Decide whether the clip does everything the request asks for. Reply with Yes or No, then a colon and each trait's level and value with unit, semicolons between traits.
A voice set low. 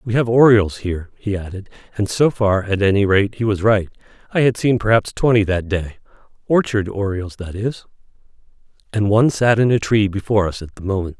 Yes: low, 105 Hz